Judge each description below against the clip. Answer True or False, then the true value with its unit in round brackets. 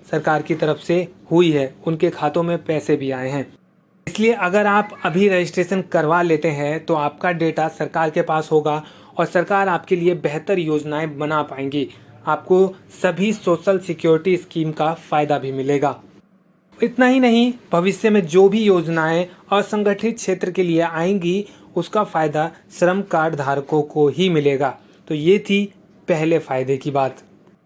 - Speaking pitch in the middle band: True (170 Hz)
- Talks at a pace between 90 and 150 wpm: False (160 wpm)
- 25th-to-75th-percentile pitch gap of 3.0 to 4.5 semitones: True (3.7 semitones)